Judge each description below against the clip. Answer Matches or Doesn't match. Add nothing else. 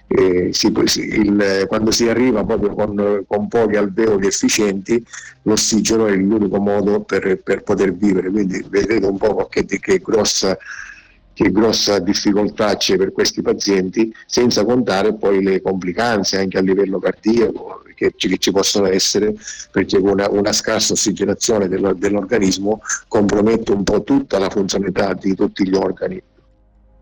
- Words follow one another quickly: Doesn't match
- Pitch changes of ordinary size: Doesn't match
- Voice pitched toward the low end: Matches